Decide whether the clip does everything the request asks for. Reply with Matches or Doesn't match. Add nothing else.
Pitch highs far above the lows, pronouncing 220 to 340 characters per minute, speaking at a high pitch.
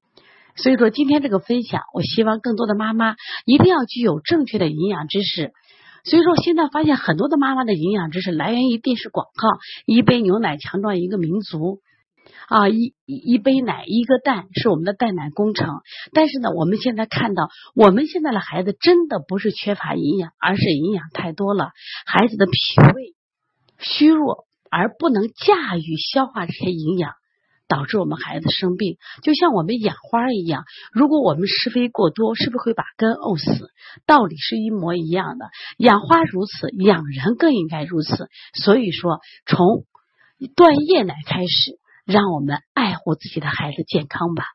Matches